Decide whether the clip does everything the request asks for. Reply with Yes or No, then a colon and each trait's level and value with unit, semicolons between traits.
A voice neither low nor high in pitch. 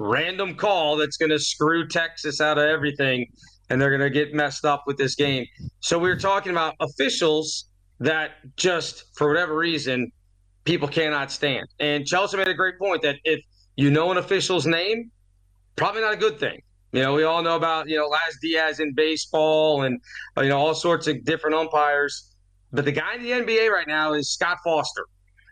Yes: medium, 150 Hz